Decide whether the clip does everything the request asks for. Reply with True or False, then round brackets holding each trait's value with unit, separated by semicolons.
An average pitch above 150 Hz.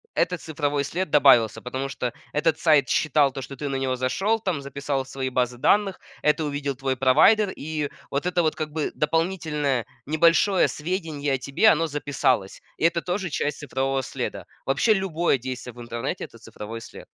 False (145 Hz)